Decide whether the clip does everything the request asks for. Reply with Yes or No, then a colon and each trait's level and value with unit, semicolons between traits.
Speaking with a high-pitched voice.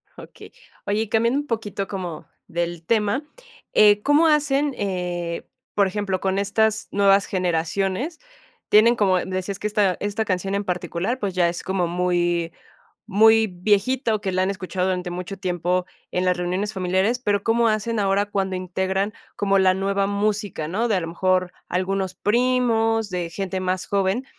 Yes: high, 195 Hz